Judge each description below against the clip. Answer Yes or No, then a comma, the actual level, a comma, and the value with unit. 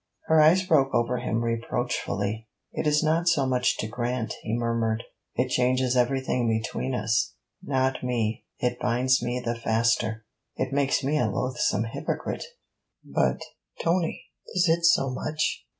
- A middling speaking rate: Yes, average, 150 wpm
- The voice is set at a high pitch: No, low, 125 Hz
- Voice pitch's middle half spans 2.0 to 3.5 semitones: Yes, average, 2.9 semitones